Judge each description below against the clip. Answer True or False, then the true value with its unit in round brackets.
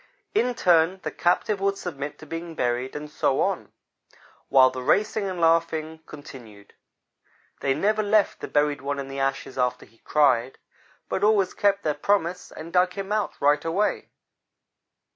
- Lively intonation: True (6.1 semitones)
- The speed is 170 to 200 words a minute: False (160 wpm)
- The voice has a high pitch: False (160 Hz)